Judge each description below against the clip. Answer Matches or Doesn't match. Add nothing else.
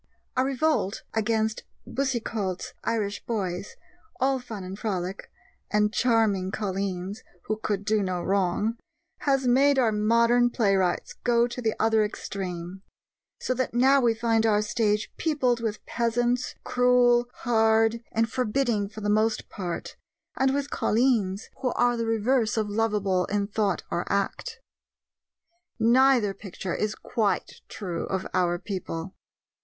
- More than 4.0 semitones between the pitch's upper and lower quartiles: Doesn't match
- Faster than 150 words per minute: Doesn't match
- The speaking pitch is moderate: Doesn't match